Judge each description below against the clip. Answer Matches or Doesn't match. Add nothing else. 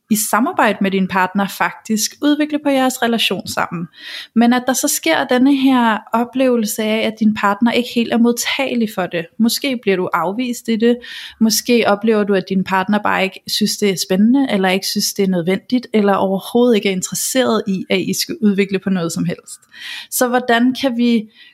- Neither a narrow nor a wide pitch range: Matches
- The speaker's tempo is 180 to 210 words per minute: Matches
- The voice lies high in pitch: Matches